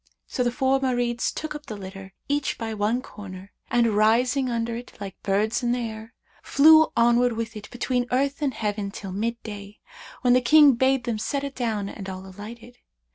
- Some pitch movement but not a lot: Yes, average, 3.4 semitones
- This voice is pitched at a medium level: No, high, 235 Hz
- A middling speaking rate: Yes, average, 190 wpm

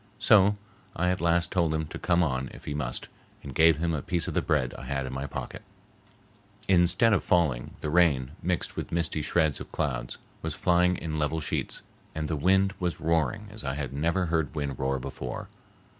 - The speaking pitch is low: Yes, very low, 80 Hz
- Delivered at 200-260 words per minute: Yes, fast, 205 wpm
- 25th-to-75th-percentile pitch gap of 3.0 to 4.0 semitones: Yes, average, 3.7 semitones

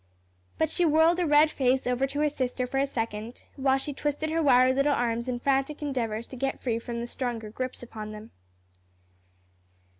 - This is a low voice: No, very high, 260 Hz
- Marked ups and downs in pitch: No, average, 3.4 semitones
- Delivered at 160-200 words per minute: Yes, average, 190 wpm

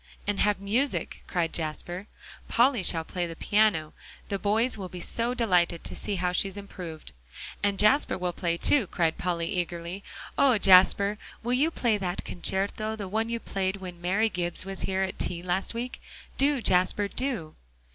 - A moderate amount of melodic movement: Yes, average, 3.6 semitones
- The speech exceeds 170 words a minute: Yes, average, 180 wpm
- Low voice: No, high, 195 Hz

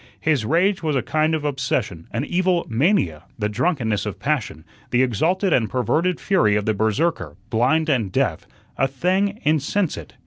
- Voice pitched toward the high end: No, low, 135 Hz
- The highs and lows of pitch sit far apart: Yes, wide, 7.4 semitones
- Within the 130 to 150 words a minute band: No, average, 165 wpm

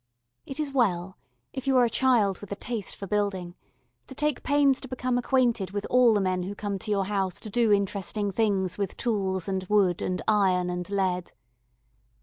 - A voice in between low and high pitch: No, high, 205 Hz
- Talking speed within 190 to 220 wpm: Yes, average, 195 wpm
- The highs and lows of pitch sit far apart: No, average, 4.4 semitones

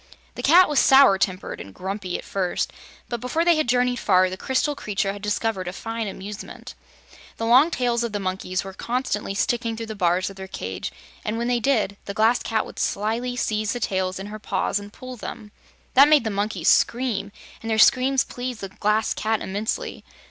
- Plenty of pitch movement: No, average, 3.9 semitones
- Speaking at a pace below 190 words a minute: No, fast, 205 wpm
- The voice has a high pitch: Yes, high, 215 Hz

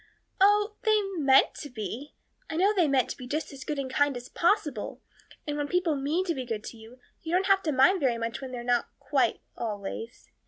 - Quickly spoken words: Yes, fast, 210 wpm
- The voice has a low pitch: No, very high, 285 Hz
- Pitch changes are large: Yes, wide, 6.5 semitones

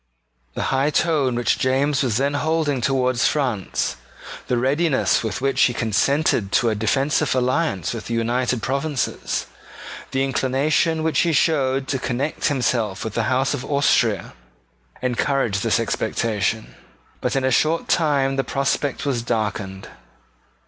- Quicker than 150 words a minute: No, average, 140 wpm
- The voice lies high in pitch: No, low, 130 Hz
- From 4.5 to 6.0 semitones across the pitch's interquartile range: No, average, 3.3 semitones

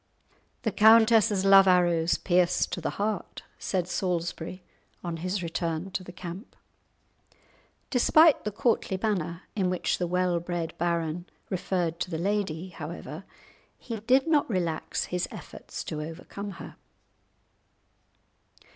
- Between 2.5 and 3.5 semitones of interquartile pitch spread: Yes, average, 3.0 semitones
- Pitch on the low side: No, medium, 180 Hz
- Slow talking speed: Yes, slow, 130 wpm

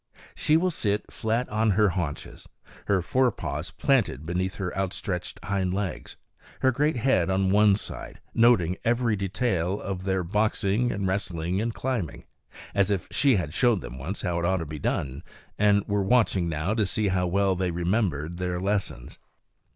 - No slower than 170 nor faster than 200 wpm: Yes, average, 175 wpm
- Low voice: Yes, very low, 95 Hz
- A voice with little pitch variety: No, average, 3.4 semitones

